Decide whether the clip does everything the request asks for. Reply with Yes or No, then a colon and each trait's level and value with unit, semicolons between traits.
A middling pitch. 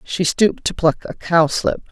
Yes: medium, 170 Hz